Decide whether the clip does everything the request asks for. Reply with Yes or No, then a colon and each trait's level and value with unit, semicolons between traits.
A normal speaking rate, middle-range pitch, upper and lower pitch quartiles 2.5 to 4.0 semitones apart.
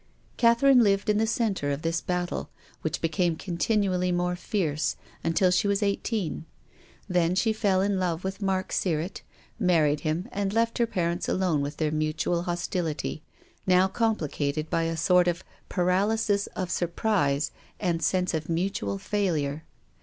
Yes: average, 155 wpm; medium, 180 Hz; average, 3.6 semitones